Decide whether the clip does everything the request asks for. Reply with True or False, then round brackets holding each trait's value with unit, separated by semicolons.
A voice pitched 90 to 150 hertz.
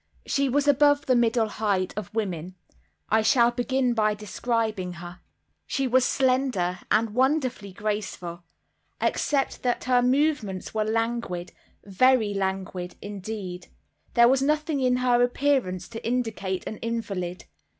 False (225 Hz)